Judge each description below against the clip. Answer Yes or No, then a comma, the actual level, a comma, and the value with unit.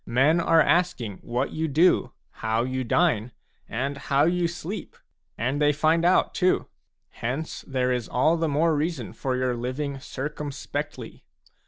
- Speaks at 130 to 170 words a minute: Yes, average, 150 wpm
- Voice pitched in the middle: Yes, medium, 145 Hz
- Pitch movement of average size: Yes, average, 4.3 semitones